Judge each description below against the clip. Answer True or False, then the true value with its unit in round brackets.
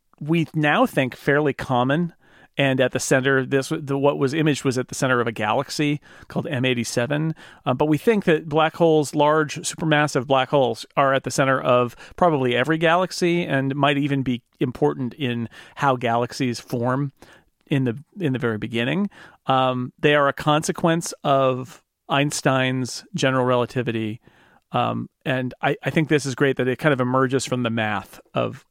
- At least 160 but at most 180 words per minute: True (175 wpm)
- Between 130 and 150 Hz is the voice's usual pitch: True (135 Hz)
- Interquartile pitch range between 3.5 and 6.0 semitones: False (3.0 semitones)